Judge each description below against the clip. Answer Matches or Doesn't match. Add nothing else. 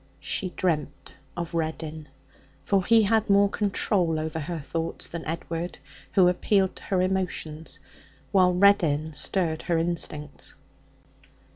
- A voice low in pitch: Doesn't match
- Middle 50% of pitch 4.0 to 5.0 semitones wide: Doesn't match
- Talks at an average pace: Doesn't match